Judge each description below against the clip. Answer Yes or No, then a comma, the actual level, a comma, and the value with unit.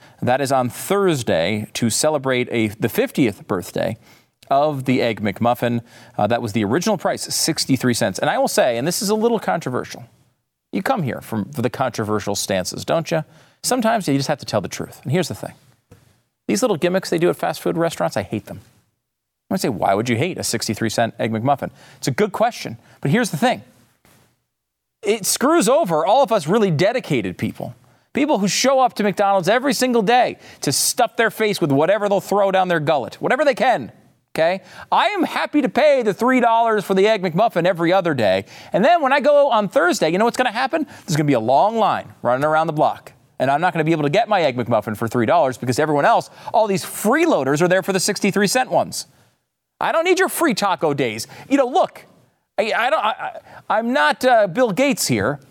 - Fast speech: Yes, fast, 220 wpm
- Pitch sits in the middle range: Yes, medium, 180 Hz